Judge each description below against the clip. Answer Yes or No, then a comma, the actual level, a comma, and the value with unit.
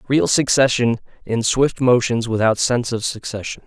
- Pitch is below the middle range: Yes, low, 120 Hz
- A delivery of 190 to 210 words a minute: No, average, 145 wpm